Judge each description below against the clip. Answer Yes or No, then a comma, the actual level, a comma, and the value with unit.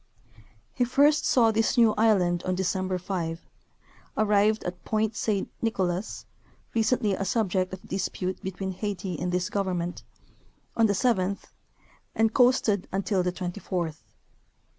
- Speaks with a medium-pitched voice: No, high, 195 Hz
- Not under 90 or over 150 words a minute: Yes, slow, 135 wpm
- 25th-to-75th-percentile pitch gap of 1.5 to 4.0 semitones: Yes, average, 3.2 semitones